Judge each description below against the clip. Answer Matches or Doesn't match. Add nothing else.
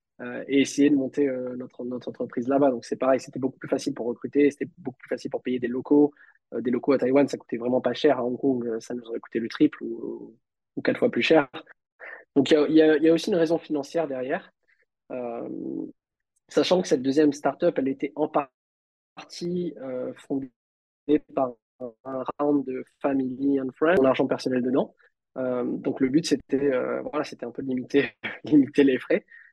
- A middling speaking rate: Matches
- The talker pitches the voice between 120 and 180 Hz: Matches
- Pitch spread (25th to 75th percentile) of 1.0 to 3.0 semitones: Matches